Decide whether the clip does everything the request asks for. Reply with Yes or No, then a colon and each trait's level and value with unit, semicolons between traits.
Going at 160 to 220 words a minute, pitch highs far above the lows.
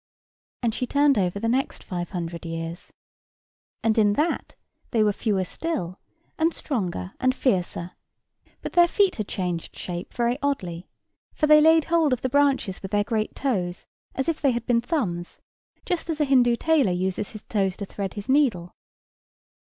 Yes: average, 175 wpm; wide, 7.5 semitones